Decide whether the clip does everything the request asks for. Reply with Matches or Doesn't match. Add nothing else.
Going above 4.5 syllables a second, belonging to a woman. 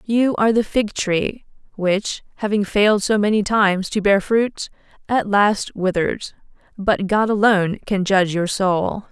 Doesn't match